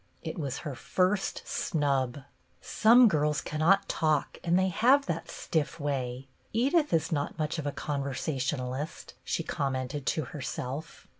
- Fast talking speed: No, average, 150 wpm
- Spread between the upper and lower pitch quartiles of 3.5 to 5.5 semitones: Yes, average, 4.0 semitones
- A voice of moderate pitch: Yes, medium, 150 Hz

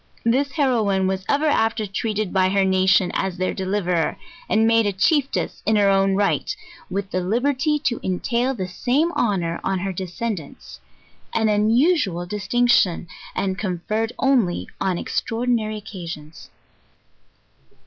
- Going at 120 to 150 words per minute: Yes, average, 140 wpm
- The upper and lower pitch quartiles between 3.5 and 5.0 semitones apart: Yes, average, 4.0 semitones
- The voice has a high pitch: Yes, high, 205 Hz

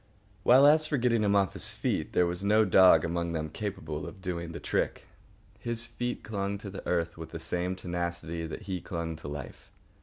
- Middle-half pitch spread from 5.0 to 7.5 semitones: No, average, 3.8 semitones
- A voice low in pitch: Yes, very low, 90 Hz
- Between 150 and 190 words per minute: No, fast, 205 wpm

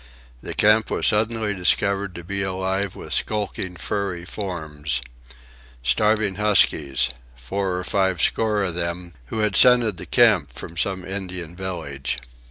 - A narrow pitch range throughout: No, average, 3.7 semitones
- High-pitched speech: No, very low, 95 Hz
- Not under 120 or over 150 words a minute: Yes, slow, 135 wpm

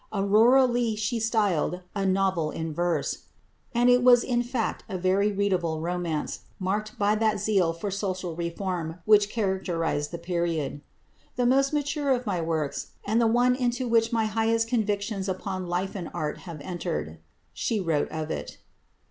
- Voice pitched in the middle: No, high, 195 Hz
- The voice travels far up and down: No, average, 4.8 semitones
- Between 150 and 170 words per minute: Yes, average, 165 wpm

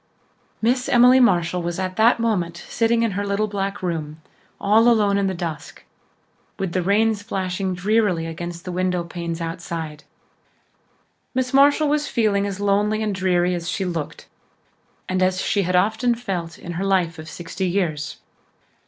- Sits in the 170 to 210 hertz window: Yes, high, 190 Hz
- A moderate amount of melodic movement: Yes, average, 3.8 semitones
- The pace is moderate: Yes, average, 160 wpm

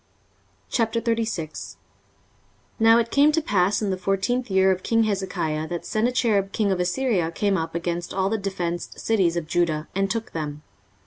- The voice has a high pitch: Yes, high, 195 Hz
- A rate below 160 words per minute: No, average, 165 wpm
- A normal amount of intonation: Yes, average, 4.5 semitones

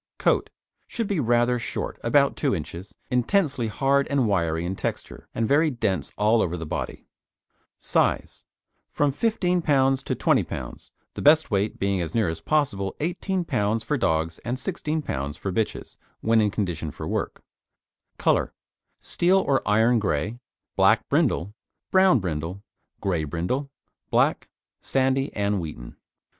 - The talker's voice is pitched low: Yes, low, 115 Hz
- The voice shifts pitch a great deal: Yes, wide, 7.4 semitones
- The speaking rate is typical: Yes, average, 150 wpm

